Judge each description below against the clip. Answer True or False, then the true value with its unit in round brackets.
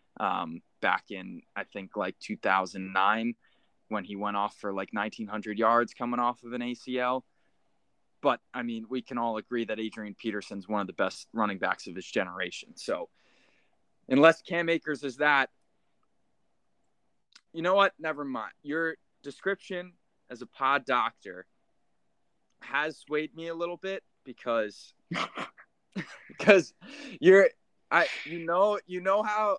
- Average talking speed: True (145 wpm)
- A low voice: True (125 Hz)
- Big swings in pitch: True (7.9 semitones)